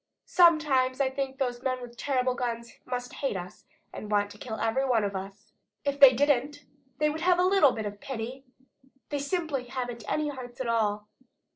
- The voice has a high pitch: Yes, very high, 255 Hz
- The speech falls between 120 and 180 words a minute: No, average, 195 wpm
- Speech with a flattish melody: No, average, 3.7 semitones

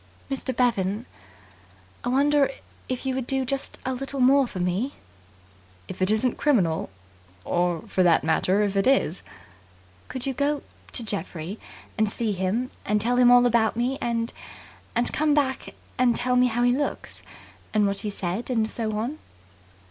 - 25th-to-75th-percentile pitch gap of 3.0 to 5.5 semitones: Yes, average, 4.3 semitones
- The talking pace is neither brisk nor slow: Yes, average, 170 wpm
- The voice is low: No, high, 240 Hz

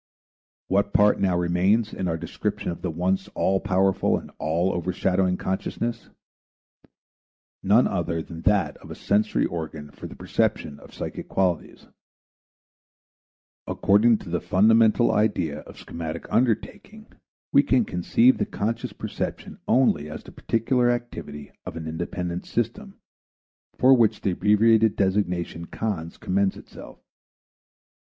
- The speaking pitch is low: Yes, very low, 95 Hz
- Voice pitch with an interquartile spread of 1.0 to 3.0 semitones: No, average, 4.5 semitones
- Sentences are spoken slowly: Yes, slow, 130 wpm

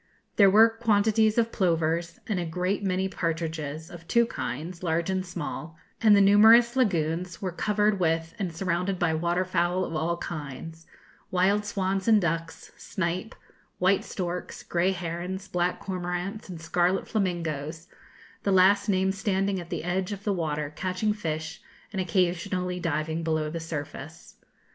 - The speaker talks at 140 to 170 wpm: Yes, average, 155 wpm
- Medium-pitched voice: Yes, medium, 180 Hz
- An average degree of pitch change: Yes, average, 3.0 semitones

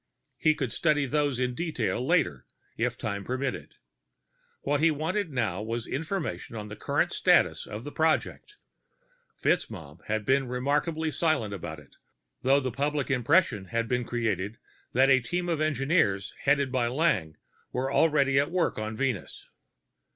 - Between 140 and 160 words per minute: Yes, average, 150 wpm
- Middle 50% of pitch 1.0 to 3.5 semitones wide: No, wide, 5.5 semitones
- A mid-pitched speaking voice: No, low, 130 Hz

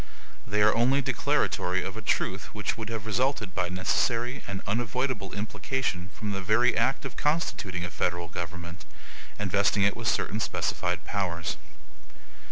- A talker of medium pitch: No, low, 105 Hz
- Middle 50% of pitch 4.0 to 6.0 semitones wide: Yes, average, 4.4 semitones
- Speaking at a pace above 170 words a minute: No, average, 155 wpm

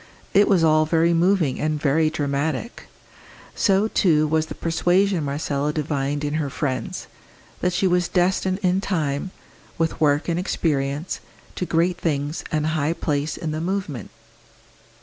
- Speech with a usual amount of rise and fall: Yes, average, 3.4 semitones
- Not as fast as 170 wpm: Yes, average, 150 wpm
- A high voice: No, medium, 160 Hz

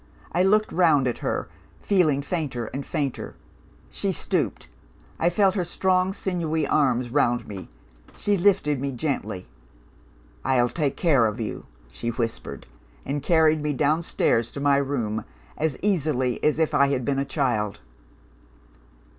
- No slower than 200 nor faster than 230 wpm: No, average, 145 wpm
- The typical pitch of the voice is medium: Yes, medium, 145 Hz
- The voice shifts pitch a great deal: No, average, 4.9 semitones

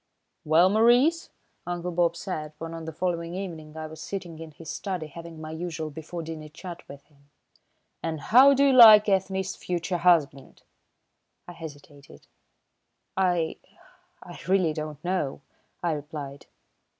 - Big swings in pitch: No, average, 3.0 semitones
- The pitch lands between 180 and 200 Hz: No, medium, 165 Hz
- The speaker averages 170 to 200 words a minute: No, average, 145 wpm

